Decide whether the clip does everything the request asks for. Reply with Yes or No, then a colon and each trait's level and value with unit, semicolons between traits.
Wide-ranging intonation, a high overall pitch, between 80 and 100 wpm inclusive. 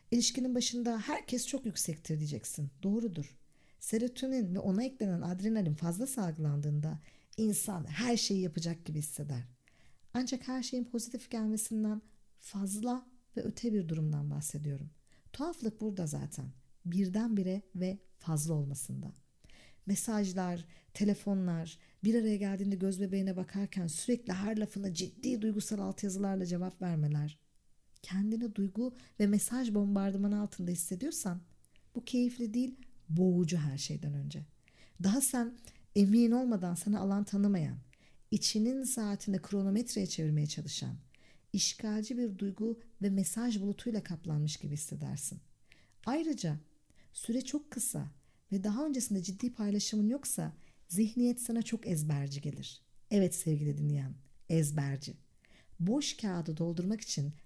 No: wide, 6.2 semitones; high, 195 Hz; average, 115 wpm